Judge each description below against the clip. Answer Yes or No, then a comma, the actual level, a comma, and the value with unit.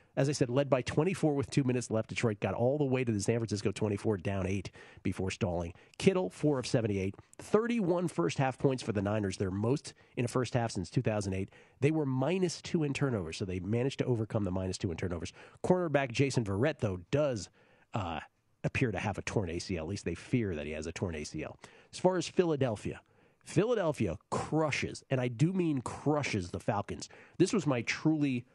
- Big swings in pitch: Yes, wide, 6.1 semitones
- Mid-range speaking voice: No, low, 120 Hz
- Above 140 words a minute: Yes, fast, 205 wpm